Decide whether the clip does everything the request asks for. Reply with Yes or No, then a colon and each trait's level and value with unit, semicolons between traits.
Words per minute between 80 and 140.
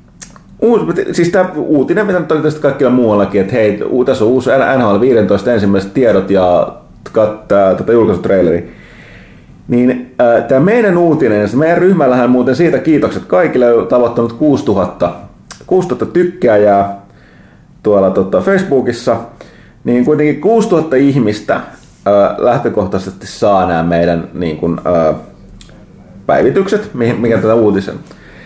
Yes: average, 120 wpm